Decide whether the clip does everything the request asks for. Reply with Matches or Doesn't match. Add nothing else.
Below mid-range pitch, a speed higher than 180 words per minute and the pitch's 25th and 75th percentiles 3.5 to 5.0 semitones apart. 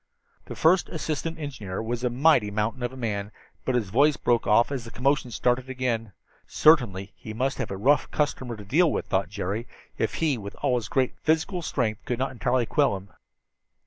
Matches